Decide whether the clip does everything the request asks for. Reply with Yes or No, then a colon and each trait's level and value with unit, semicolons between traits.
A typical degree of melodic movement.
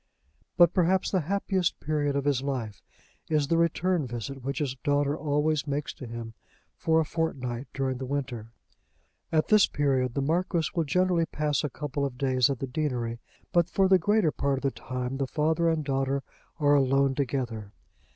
Yes: average, 3.5 semitones